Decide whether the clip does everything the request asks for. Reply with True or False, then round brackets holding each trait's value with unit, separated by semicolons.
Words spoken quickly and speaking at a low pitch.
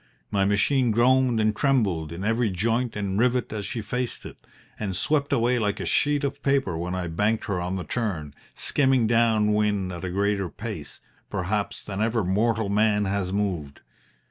False (180 wpm; 105 Hz)